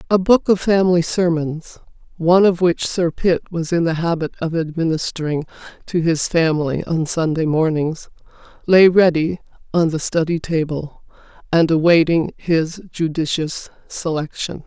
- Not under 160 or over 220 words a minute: No, slow, 135 wpm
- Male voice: No, female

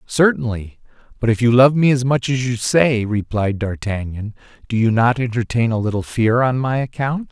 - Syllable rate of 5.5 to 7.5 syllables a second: No, 5.0 syllables/s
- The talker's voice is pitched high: No, low, 120 Hz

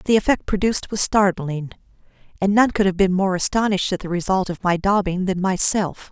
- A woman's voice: Yes, female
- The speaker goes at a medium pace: Yes, average, 195 wpm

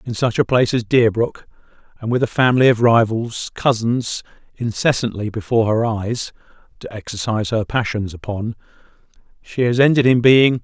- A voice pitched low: Yes, low, 115 Hz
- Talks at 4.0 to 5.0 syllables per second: No, 5.3 syllables/s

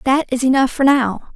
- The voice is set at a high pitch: Yes, very high, 260 Hz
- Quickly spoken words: Yes, fast, 220 wpm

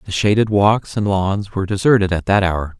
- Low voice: Yes, low, 100 Hz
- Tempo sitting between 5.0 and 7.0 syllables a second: Yes, 5.3 syllables/s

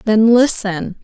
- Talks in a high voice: Yes, high, 220 Hz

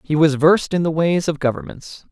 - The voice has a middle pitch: Yes, medium, 160 Hz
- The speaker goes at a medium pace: No, fast, 225 wpm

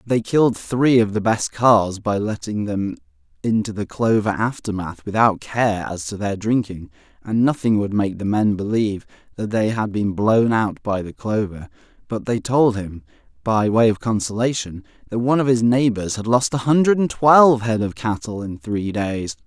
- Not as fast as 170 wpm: No, average, 190 wpm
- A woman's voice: No, male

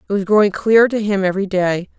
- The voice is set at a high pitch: Yes, high, 200 Hz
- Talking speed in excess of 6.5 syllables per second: Yes, 6.9 syllables/s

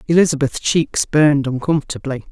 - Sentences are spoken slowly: Yes, slow, 105 wpm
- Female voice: Yes, female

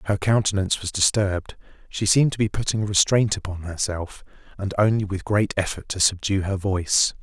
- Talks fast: No, average, 185 wpm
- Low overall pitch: Yes, low, 100 Hz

